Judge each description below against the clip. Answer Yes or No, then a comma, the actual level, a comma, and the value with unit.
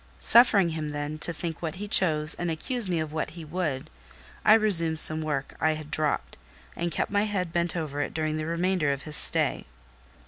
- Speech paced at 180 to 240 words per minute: Yes, fast, 205 wpm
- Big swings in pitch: No, average, 2.9 semitones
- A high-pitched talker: No, medium, 160 Hz